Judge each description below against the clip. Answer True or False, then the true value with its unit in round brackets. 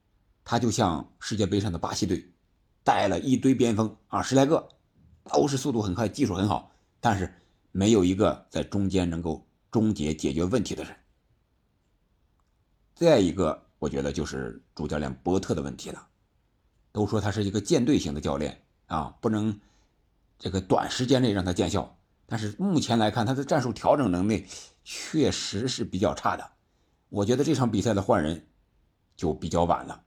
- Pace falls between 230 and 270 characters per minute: True (255 characters per minute)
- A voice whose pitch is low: True (100 Hz)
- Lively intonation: False (4.4 semitones)